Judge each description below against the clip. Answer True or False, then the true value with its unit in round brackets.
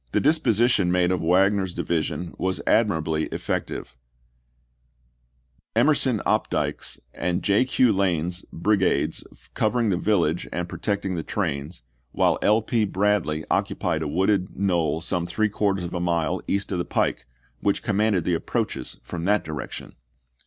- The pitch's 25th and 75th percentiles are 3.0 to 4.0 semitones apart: True (3.5 semitones)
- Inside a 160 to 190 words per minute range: False (145 wpm)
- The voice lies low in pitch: True (95 Hz)